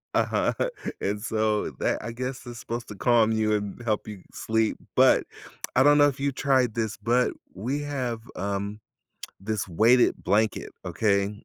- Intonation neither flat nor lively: Yes, average, 3.0 semitones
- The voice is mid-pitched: No, low, 110 Hz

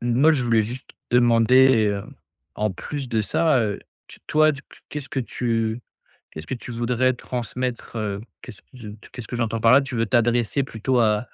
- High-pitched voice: No, low, 120 Hz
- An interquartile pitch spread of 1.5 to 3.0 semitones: Yes, narrow, 2.6 semitones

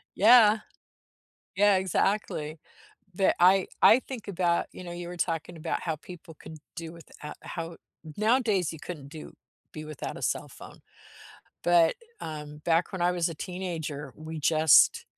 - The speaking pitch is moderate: Yes, medium, 170 Hz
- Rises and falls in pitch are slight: No, average, 3.1 semitones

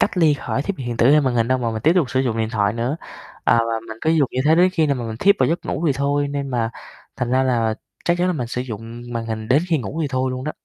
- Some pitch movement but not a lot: Yes, average, 4.5 semitones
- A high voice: No, low, 130 Hz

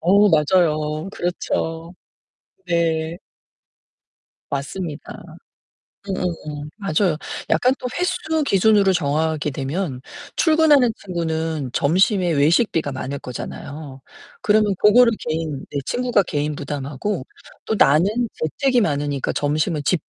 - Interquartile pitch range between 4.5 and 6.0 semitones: Yes, average, 5.2 semitones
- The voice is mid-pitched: Yes, medium, 165 Hz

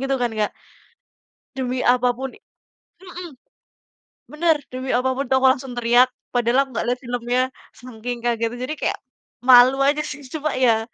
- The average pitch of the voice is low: No, very high, 255 Hz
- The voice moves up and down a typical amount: No, narrow, 1.9 semitones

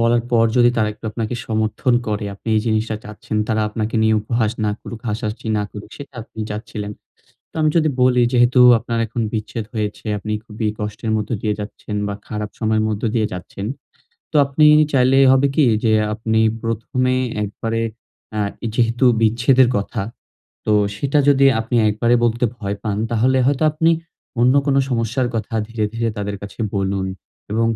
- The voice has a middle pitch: No, low, 115 Hz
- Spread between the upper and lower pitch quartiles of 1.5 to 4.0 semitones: Yes, narrow, 2.5 semitones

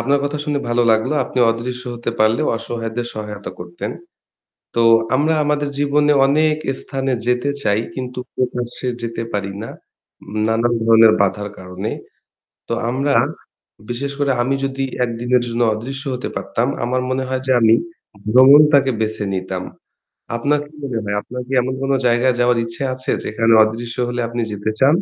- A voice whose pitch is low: Yes, low, 120 Hz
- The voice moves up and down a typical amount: Yes, average, 3.1 semitones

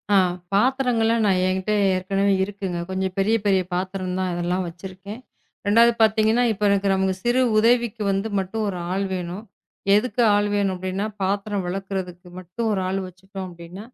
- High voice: Yes, high, 195 Hz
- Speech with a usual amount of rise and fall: No, narrow, 2.3 semitones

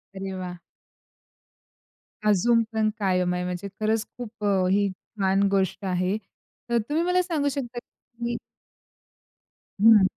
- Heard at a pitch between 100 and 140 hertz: No, high, 210 Hz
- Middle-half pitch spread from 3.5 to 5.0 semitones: Yes, average, 3.8 semitones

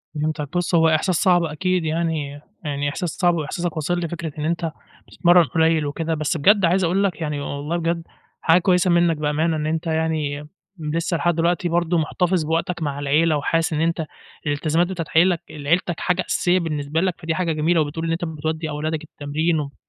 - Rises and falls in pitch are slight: Yes, narrow, 2.1 semitones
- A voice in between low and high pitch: Yes, medium, 165 Hz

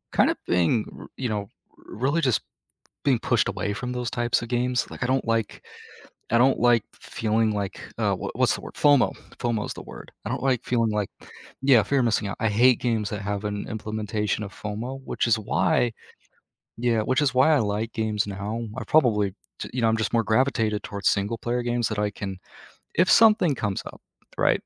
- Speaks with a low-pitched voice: Yes, low, 115 Hz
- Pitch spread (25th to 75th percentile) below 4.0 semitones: Yes, average, 2.9 semitones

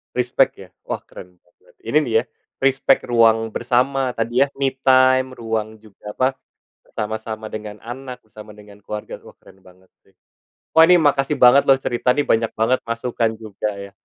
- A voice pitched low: Yes, low, 115 Hz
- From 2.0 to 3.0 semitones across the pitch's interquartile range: No, average, 3.5 semitones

